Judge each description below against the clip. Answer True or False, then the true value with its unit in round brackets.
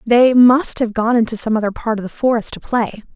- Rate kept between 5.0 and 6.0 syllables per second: True (5.5 syllables/s)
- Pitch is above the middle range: True (230 Hz)